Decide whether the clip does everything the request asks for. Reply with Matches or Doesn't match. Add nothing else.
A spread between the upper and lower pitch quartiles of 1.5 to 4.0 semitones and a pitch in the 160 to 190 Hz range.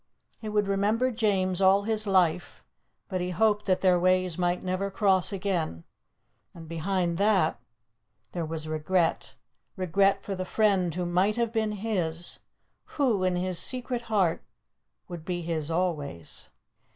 Matches